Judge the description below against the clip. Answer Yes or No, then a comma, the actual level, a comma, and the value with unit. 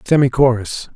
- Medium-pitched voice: No, low, 130 Hz